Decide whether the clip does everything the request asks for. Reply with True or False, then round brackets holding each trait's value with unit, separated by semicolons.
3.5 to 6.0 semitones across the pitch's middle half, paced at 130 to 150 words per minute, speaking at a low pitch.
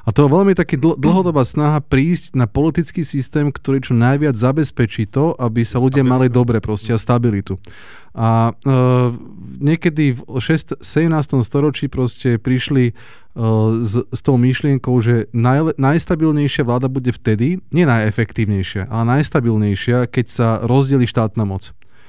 True (4.2 semitones; 145 wpm; 125 Hz)